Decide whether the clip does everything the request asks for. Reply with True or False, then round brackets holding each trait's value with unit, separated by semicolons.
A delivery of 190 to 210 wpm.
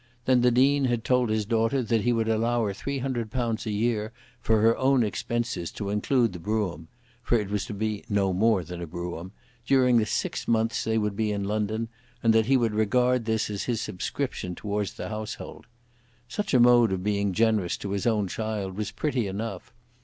True (200 wpm)